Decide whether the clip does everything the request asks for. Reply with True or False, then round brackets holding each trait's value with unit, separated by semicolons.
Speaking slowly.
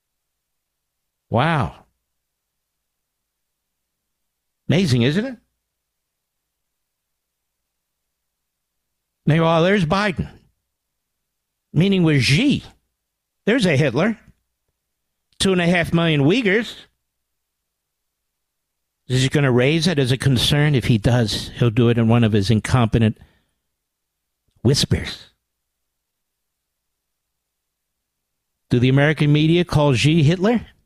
True (90 wpm)